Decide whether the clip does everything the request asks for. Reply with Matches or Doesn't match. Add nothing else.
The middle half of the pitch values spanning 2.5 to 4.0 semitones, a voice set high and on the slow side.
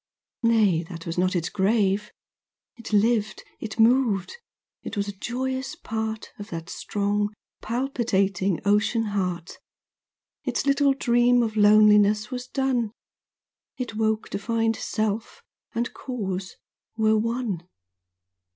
Matches